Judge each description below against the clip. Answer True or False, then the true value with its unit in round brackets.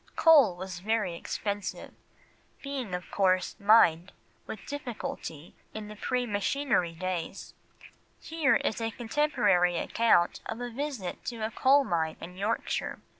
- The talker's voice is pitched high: True (210 Hz)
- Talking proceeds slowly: True (130 wpm)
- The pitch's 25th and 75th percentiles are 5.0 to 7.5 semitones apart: True (5.5 semitones)